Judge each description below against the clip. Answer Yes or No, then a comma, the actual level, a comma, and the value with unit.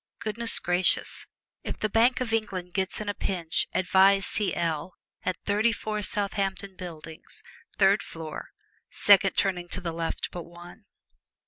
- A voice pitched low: No, high, 190 Hz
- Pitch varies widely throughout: No, average, 2.9 semitones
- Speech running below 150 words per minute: Yes, average, 140 wpm